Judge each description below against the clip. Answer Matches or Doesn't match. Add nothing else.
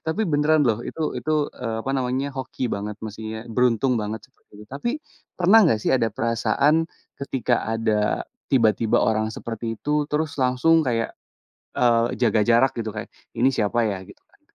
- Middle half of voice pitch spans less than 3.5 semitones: Doesn't match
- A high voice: Doesn't match